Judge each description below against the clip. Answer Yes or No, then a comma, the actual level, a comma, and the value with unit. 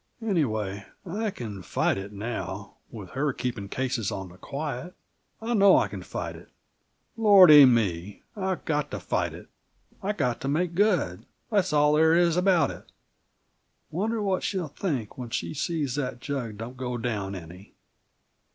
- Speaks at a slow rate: No, average, 160 wpm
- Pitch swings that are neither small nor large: No, wide, 8.9 semitones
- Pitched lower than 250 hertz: Yes, low, 135 Hz